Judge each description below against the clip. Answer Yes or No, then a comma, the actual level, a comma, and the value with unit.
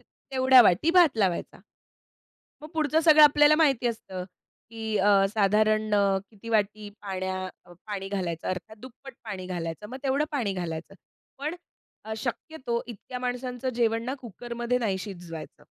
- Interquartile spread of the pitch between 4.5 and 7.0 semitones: Yes, average, 4.9 semitones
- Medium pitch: No, high, 220 Hz